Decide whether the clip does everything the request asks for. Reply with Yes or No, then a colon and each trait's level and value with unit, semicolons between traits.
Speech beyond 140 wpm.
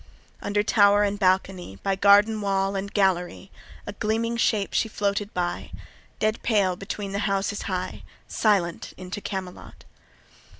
No: slow, 135 wpm